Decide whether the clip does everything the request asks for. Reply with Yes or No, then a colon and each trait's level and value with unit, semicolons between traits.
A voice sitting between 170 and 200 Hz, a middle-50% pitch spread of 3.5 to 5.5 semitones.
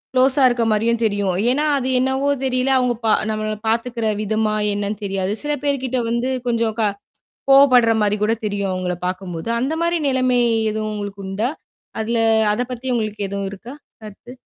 No: high, 225 Hz; average, 3.8 semitones